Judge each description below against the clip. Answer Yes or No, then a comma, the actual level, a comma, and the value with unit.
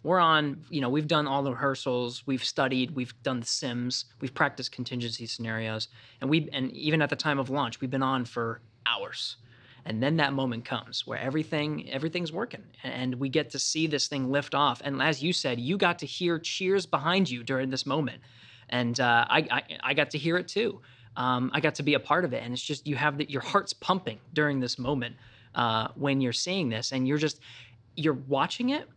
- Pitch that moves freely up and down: No, average, 3.6 semitones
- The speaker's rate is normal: No, fast, 220 wpm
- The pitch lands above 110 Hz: Yes, low, 135 Hz